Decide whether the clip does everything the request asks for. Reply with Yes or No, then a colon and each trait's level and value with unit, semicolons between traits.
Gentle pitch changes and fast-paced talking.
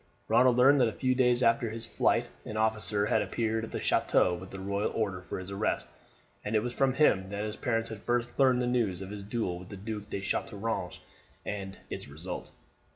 No: average, 3.7 semitones; fast, 220 wpm